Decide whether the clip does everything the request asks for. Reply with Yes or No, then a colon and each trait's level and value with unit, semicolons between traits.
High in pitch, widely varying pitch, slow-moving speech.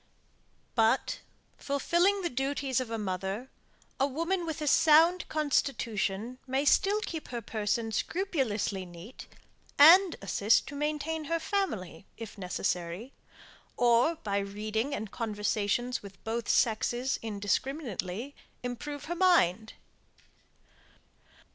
Yes: high, 245 Hz; wide, 6.5 semitones; slow, 110 wpm